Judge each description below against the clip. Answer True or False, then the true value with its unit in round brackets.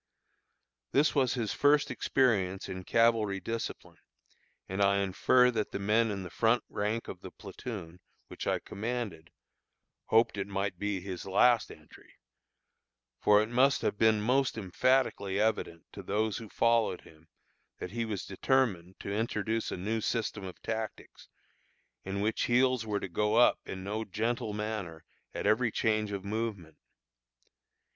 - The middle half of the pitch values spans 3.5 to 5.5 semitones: False (2.9 semitones)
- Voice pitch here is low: True (105 Hz)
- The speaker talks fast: False (150 wpm)